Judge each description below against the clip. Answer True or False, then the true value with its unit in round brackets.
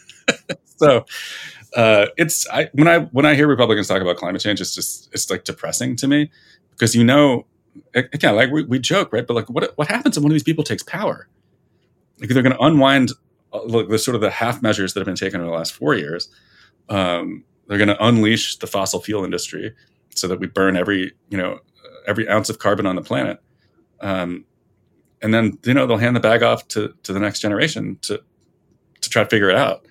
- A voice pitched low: True (115 Hz)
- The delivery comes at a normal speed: False (220 wpm)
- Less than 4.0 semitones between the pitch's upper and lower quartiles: False (5.1 semitones)